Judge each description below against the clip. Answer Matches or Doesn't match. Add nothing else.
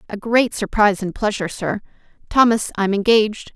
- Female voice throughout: Matches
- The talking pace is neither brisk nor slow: Matches